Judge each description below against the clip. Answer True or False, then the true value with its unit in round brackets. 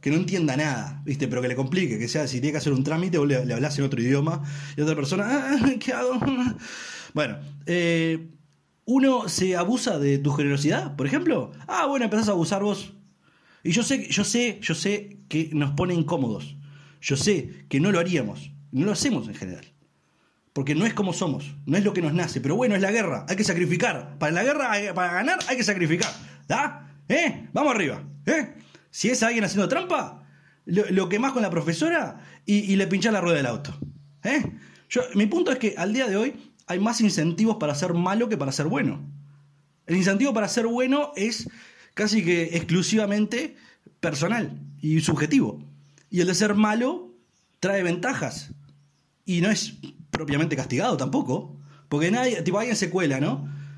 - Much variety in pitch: True (6.6 semitones)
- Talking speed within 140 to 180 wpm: False (190 wpm)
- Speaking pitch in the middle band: True (175 Hz)